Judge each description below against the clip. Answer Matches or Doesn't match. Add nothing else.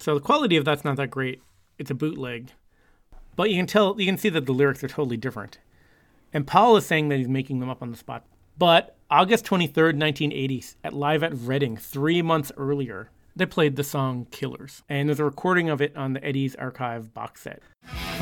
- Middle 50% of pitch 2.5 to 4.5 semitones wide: Matches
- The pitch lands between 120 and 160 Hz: Matches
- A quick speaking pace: Matches